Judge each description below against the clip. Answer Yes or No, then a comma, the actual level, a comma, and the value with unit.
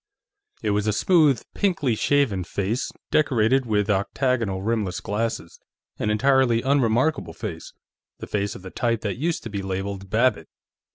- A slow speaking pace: No, average, 150 wpm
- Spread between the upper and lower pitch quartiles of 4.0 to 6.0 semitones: Yes, average, 4.7 semitones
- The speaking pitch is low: Yes, low, 110 Hz